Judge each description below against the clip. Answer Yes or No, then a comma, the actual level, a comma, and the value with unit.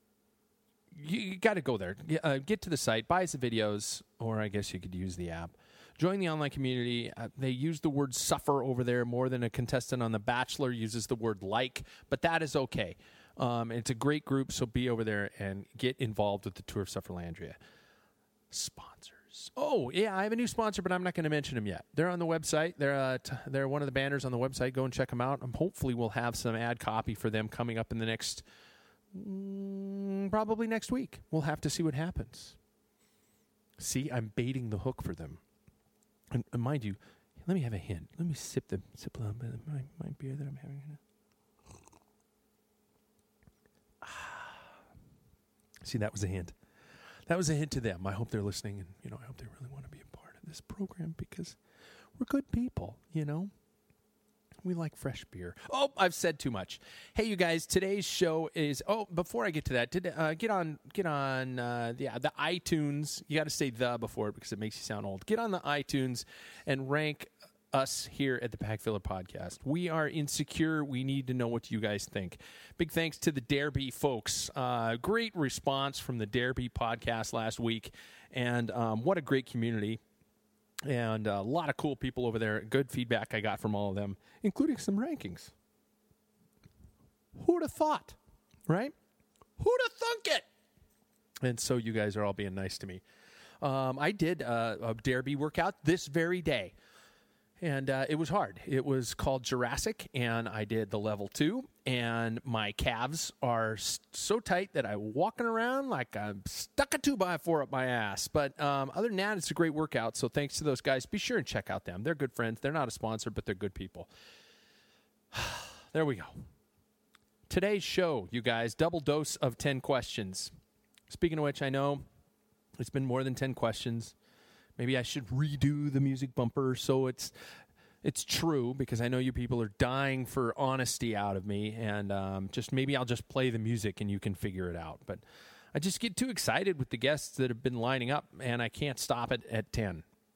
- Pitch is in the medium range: No, low, 130 Hz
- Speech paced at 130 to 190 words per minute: No, fast, 205 wpm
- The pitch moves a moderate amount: No, wide, 5.7 semitones